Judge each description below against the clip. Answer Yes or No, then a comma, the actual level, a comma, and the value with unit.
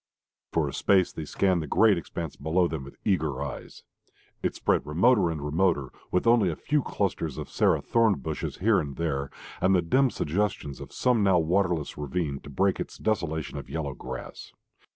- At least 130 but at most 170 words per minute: No, average, 185 wpm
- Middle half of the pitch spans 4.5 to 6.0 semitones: Yes, average, 5.0 semitones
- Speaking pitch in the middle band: No, very low, 85 Hz